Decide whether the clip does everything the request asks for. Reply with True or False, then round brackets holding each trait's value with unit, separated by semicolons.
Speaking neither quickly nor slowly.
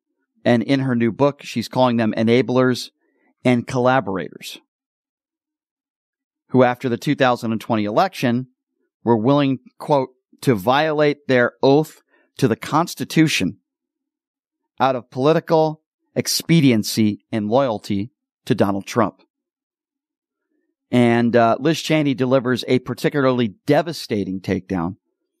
False (105 wpm)